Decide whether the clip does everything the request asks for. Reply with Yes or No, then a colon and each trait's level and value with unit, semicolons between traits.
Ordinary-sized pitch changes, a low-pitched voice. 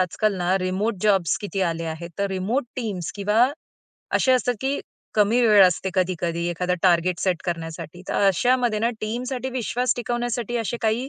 No: average, 5.0 semitones; high, 205 Hz